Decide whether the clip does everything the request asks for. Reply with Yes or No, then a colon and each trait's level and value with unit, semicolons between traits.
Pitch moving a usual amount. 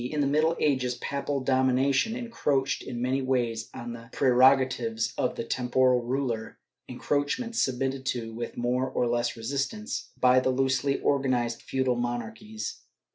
No: narrow, 2.3 semitones